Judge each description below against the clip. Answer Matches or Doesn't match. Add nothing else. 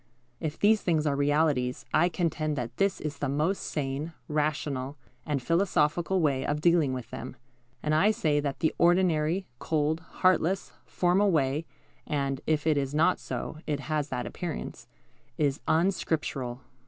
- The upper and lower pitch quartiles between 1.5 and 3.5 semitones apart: Matches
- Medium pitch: Matches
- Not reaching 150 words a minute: Doesn't match